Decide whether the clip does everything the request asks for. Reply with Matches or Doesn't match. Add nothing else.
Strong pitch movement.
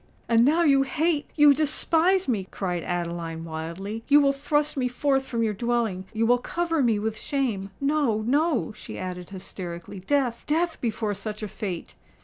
Matches